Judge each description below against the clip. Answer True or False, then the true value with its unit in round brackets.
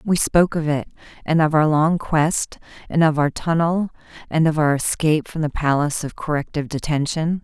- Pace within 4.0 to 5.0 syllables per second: False (5.4 syllables/s)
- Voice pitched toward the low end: False (155 Hz)